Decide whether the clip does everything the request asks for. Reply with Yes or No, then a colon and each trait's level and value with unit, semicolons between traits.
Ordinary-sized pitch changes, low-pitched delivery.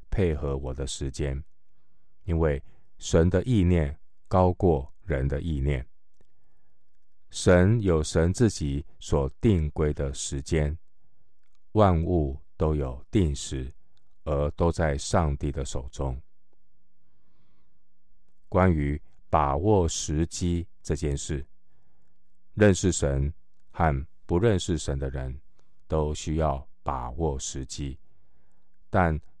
Yes: average, 4.4 semitones; very low, 80 Hz